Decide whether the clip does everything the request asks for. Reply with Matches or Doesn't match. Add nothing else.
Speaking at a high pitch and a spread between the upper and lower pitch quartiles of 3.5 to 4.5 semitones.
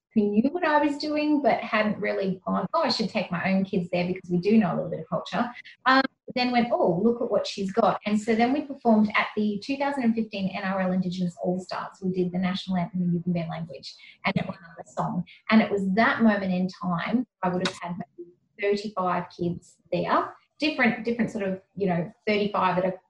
Matches